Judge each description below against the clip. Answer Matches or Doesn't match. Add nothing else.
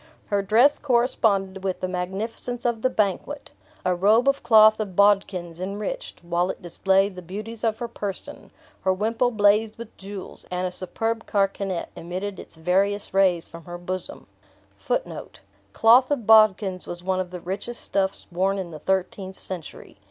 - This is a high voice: Matches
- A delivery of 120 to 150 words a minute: Doesn't match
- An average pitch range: Matches